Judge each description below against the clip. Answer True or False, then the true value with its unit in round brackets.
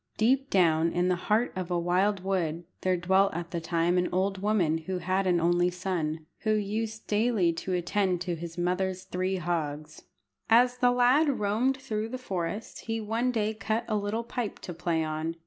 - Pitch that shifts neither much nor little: True (3.9 semitones)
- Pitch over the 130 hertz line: True (185 Hz)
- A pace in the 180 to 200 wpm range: True (190 wpm)